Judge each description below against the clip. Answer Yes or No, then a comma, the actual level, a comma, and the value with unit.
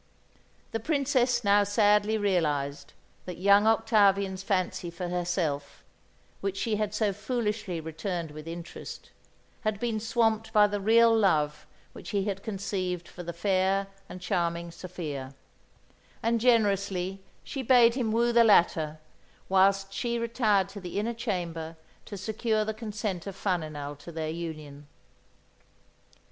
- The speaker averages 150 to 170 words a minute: No, slow, 135 wpm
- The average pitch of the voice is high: Yes, high, 195 Hz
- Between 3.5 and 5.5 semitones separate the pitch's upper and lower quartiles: Yes, average, 4.1 semitones